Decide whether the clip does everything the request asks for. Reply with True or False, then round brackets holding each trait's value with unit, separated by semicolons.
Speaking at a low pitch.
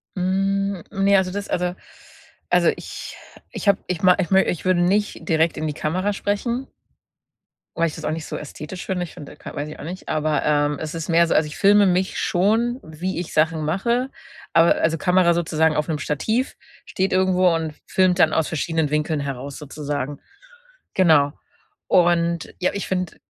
False (170 Hz)